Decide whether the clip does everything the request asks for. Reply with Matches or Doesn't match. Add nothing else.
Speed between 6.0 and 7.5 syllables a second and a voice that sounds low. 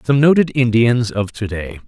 Doesn't match